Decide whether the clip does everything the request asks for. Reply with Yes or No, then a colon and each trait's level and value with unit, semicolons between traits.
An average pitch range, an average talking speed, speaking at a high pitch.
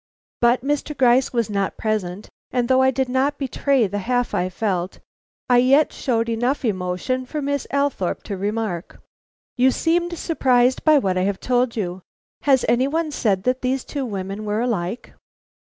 Yes: average, 4.6 semitones; average, 175 wpm; high, 245 Hz